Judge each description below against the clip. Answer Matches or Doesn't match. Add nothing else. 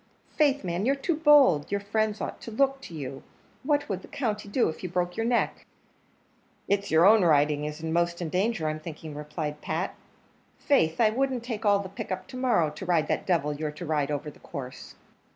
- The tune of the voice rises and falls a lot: Matches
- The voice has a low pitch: Doesn't match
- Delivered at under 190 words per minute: Doesn't match